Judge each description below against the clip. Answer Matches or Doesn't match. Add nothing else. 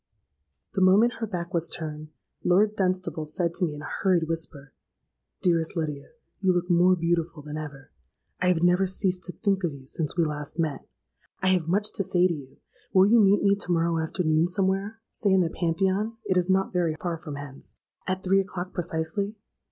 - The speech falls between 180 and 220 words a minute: Matches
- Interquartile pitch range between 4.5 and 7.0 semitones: Doesn't match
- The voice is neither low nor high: Matches